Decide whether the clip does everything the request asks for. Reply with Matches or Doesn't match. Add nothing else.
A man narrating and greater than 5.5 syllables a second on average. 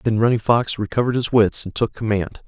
Matches